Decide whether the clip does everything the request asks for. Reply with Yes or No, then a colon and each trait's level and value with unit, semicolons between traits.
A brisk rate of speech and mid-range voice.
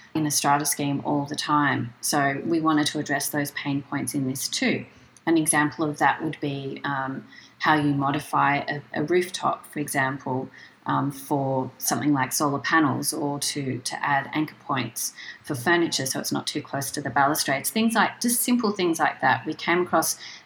No: average, 190 wpm; medium, 145 Hz